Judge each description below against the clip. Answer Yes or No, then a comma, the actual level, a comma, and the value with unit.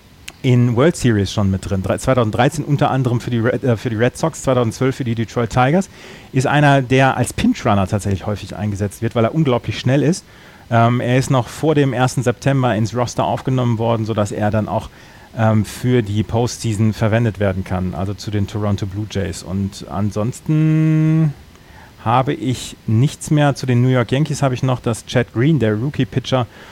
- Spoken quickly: Yes, fast, 195 wpm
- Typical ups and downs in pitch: Yes, average, 3.6 semitones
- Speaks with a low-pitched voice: Yes, low, 120 Hz